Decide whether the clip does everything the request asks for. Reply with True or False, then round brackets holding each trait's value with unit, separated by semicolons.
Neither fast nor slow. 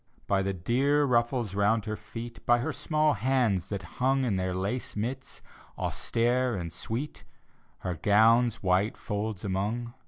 True (150 wpm)